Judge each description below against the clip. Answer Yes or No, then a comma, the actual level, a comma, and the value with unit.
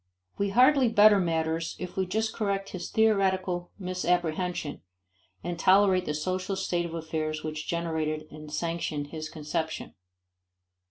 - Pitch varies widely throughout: No, average, 3.4 semitones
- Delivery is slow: Yes, slow, 130 wpm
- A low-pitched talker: No, medium, 175 Hz